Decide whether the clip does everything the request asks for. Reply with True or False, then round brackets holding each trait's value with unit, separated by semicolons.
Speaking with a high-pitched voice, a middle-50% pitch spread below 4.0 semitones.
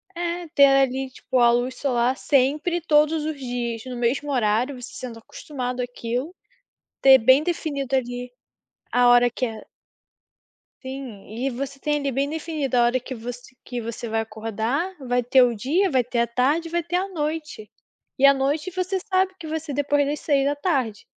True (265 Hz; 3.6 semitones)